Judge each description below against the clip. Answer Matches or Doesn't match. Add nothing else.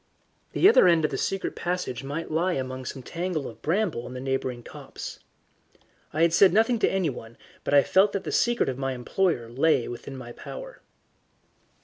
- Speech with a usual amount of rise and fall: Doesn't match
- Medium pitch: Matches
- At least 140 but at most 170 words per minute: Doesn't match